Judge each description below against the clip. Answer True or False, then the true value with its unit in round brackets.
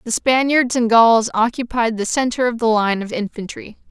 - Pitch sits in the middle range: False (230 Hz)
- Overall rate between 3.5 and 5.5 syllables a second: True (4.9 syllables/s)